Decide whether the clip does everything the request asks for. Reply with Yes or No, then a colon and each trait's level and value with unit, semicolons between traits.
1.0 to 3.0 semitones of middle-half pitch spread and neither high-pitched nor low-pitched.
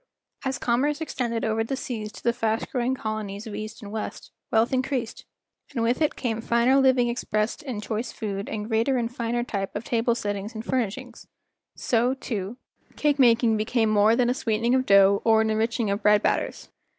No: narrow, 2.5 semitones; high, 230 Hz